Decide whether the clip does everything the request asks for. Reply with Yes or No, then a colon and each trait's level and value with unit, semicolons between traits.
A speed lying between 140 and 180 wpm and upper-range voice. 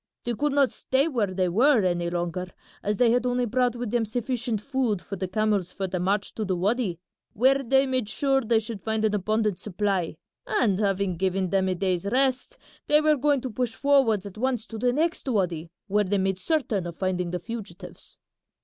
No: fast, 205 wpm; high, 215 Hz